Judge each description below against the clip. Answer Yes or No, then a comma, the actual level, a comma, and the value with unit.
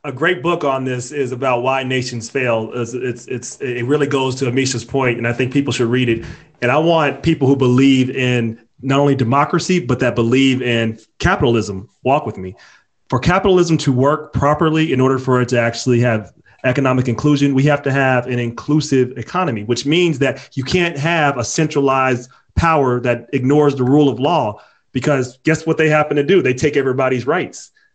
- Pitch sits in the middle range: No, low, 130 Hz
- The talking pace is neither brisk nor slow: Yes, average, 195 wpm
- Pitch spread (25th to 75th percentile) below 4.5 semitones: Yes, average, 3.0 semitones